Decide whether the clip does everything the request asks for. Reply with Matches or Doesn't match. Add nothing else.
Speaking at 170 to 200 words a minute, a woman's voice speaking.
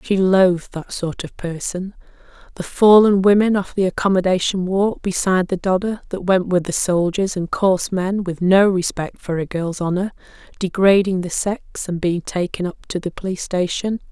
Matches